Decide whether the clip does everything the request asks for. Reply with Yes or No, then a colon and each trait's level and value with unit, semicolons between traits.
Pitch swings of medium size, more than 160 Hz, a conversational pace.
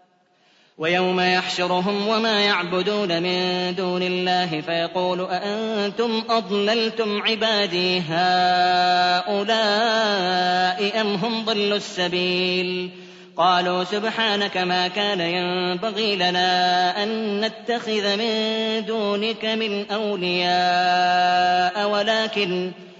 Yes: average, 3.0 semitones; medium, 185 Hz; average, 75 wpm